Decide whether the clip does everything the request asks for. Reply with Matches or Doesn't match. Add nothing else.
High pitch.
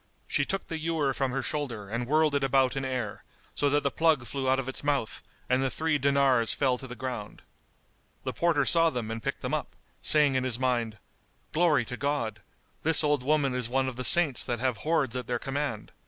Doesn't match